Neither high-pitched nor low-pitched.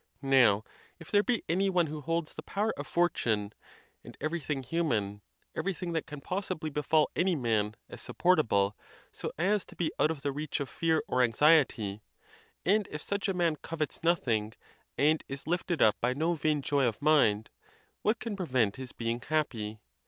Yes: medium, 150 Hz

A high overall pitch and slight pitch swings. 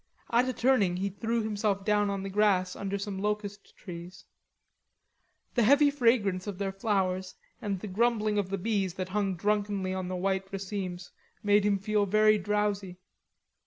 Yes: high, 200 Hz; narrow, 1.9 semitones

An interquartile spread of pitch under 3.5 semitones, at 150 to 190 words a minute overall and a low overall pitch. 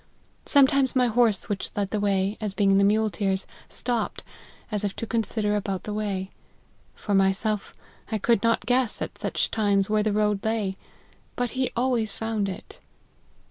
No: narrow, 2.4 semitones; average, 165 wpm; high, 210 Hz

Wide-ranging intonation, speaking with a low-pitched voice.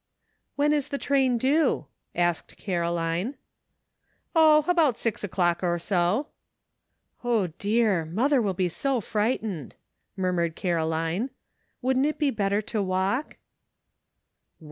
No: wide, 7.1 semitones; high, 210 Hz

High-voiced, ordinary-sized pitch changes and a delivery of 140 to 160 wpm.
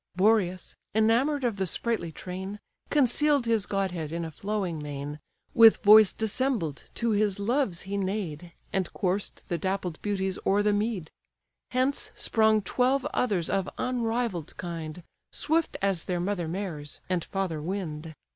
Yes: high, 195 Hz; average, 4.4 semitones; average, 145 wpm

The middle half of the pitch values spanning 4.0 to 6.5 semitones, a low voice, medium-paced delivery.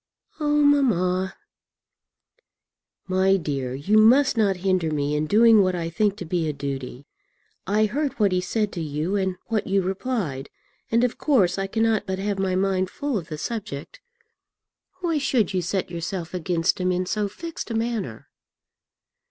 No: average, 4.4 semitones; high, 190 Hz; average, 170 wpm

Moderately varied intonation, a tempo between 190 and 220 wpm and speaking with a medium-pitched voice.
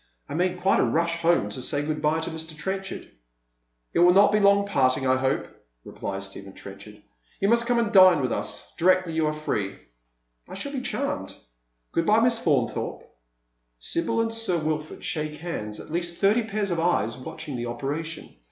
No: wide, 6.8 semitones; average, 200 wpm; medium, 165 Hz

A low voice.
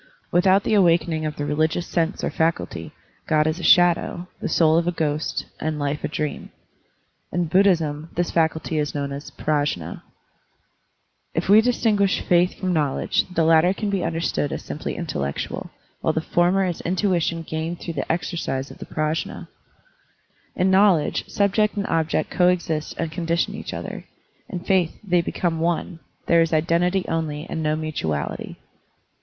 No: medium, 165 Hz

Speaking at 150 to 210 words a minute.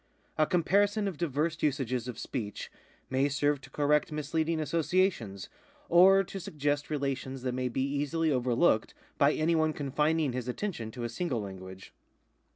Yes: average, 155 wpm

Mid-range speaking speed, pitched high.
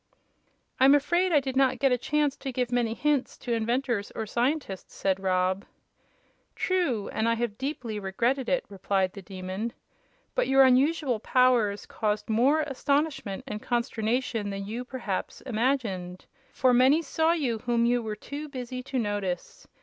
Yes: average, 155 wpm; high, 245 Hz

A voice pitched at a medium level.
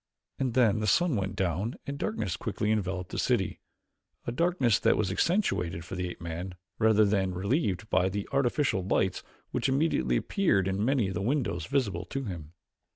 No: low, 105 Hz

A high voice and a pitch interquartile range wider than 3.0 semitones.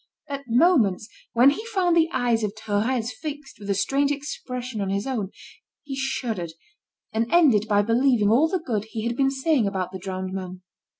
Yes: high, 235 Hz; average, 5.3 semitones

